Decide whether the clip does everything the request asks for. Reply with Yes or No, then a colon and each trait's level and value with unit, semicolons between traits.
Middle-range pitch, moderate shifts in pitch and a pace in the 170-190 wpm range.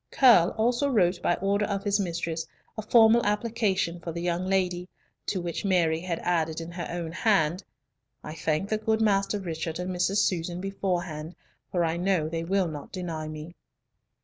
Yes: medium, 180 Hz; average, 3.0 semitones; average, 175 wpm